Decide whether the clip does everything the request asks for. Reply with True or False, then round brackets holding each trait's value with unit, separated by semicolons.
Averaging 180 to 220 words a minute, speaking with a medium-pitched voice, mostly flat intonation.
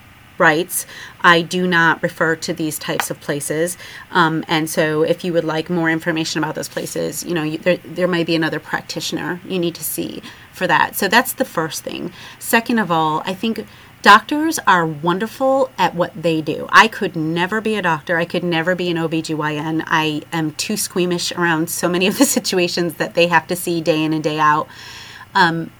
True (200 wpm; 170 Hz; 2.0 semitones)